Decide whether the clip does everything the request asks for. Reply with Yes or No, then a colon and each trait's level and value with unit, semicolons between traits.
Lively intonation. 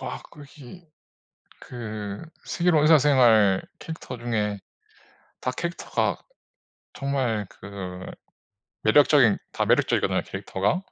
Yes: wide, 5.9 semitones